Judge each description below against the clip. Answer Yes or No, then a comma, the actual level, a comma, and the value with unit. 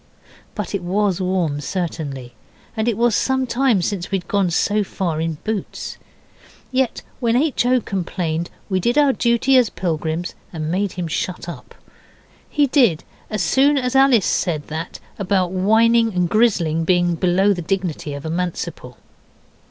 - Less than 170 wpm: Yes, average, 160 wpm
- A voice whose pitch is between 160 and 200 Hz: Yes, high, 190 Hz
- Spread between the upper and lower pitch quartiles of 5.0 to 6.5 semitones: Yes, average, 5.3 semitones